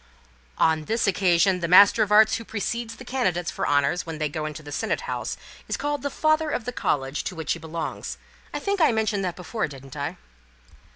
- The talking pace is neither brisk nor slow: No, fast, 220 wpm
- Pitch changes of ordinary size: No, wide, 6.5 semitones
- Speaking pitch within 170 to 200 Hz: Yes, medium, 185 Hz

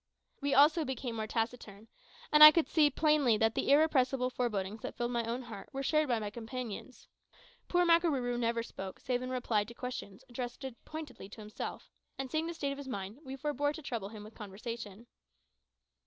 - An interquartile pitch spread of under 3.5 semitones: No, average, 4.2 semitones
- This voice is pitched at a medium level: No, very high, 250 Hz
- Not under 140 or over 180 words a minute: No, average, 190 wpm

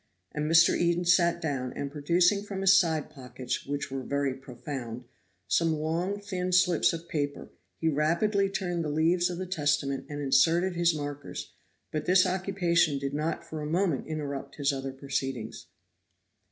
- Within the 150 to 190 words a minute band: Yes, average, 165 wpm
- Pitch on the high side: No, medium, 155 Hz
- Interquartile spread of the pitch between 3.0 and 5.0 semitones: Yes, average, 4.0 semitones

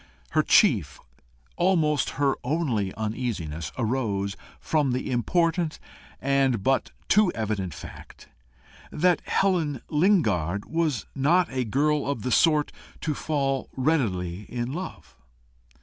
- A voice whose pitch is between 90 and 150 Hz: Yes, low, 135 Hz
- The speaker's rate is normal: No, slow, 115 wpm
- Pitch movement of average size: No, wide, 6.3 semitones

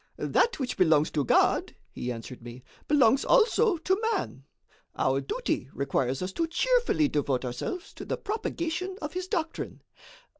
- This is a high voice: Yes, very high, 275 Hz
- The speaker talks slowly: No, average, 150 wpm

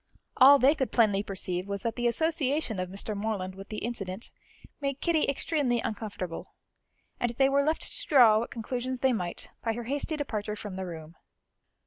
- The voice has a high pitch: Yes, high, 230 Hz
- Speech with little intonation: No, average, 5.3 semitones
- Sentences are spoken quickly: No, average, 180 wpm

